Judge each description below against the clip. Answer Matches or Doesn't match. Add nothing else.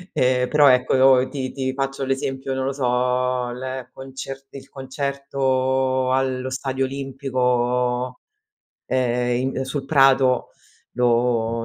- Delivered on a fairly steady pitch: Matches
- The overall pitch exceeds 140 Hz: Doesn't match